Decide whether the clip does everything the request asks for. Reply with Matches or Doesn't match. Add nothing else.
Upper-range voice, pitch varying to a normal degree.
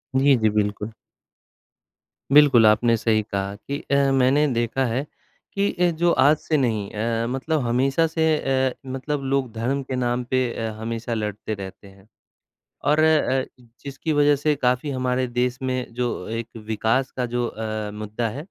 Doesn't match